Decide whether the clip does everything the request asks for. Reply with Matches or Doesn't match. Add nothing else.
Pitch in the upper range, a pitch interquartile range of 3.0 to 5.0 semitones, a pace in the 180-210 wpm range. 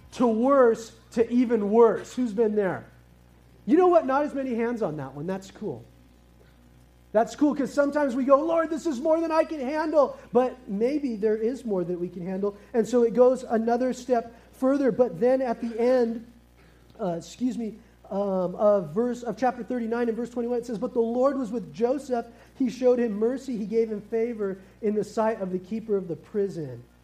Matches